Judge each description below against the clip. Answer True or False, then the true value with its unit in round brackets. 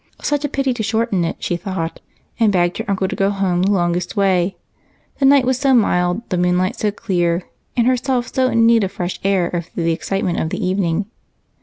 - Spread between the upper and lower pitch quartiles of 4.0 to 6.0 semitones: True (4.7 semitones)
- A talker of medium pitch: False (195 Hz)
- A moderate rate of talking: False (210 wpm)